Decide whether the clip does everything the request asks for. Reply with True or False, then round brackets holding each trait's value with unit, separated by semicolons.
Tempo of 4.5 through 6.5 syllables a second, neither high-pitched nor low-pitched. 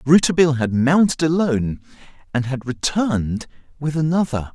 True (5.6 syllables/s; 145 Hz)